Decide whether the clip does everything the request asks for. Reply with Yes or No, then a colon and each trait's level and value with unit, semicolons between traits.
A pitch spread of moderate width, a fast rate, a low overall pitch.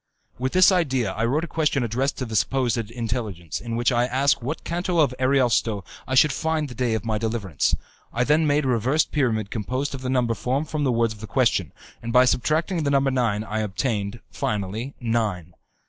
Yes: average, 3.9 semitones; fast, 210 wpm; low, 125 Hz